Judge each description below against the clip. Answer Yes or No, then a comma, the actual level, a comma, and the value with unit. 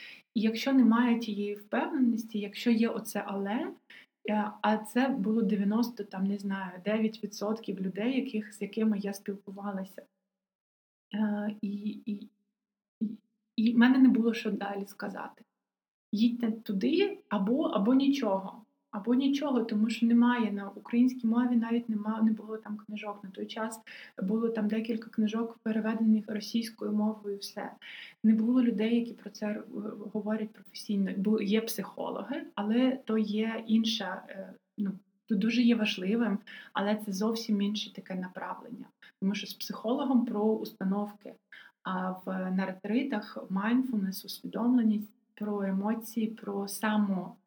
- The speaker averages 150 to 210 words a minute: No, average, 135 wpm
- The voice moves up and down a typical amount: No, narrow, 2.1 semitones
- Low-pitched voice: No, high, 215 Hz